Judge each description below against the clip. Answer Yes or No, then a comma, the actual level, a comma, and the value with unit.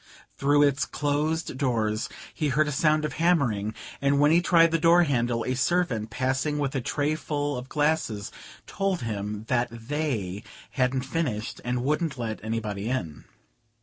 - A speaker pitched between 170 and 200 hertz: No, low, 135 Hz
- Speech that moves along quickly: No, average, 160 wpm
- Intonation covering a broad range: No, average, 4.7 semitones